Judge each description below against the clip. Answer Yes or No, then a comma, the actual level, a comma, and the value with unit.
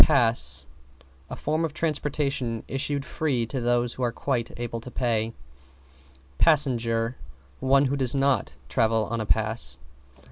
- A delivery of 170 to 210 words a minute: No, average, 140 wpm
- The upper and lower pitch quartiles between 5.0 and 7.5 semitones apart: No, average, 3.4 semitones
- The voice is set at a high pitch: No, low, 120 Hz